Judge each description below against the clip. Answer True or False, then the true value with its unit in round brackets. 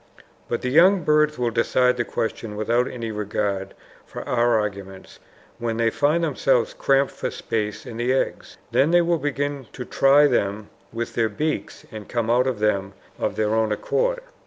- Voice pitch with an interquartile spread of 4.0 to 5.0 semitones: True (4.6 semitones)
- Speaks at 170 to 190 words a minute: True (180 wpm)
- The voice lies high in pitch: False (120 Hz)